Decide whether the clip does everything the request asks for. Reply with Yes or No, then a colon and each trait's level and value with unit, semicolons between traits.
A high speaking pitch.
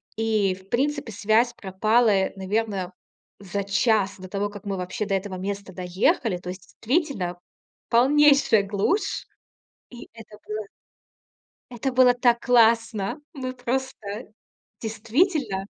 Yes: high, 215 Hz